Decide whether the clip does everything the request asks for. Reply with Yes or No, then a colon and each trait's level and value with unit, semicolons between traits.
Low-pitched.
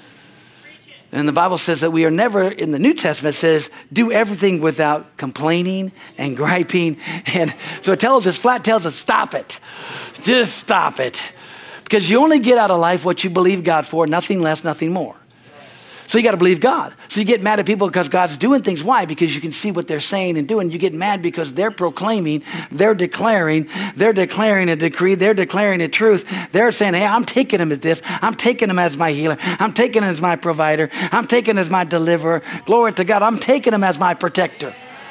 No: medium, 185 Hz